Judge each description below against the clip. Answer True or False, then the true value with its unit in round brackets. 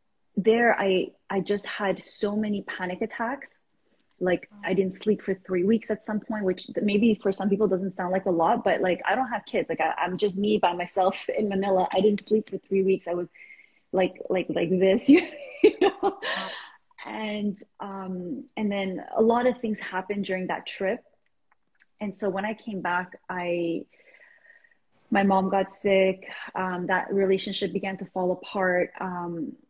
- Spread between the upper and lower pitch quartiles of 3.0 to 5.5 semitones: False (2.5 semitones)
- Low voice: False (195 Hz)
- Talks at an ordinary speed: True (180 wpm)